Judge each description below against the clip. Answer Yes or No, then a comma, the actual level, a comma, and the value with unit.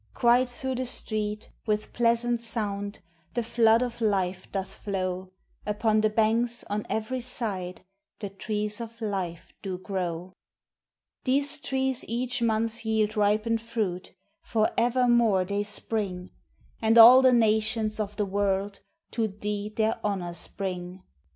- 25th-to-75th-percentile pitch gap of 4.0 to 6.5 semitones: No, average, 2.8 semitones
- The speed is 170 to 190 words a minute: No, slow, 135 wpm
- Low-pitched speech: No, high, 215 Hz